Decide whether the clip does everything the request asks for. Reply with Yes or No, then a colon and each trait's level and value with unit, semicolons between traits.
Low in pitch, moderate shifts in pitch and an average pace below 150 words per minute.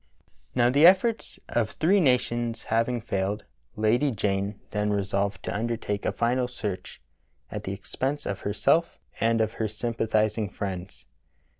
Yes: low, 110 Hz; average, 3.3 semitones; average, 140 wpm